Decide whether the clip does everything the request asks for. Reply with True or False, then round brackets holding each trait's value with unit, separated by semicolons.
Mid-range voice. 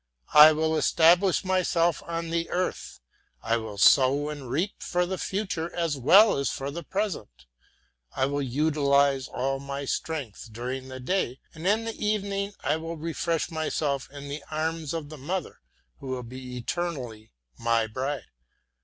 True (150 Hz)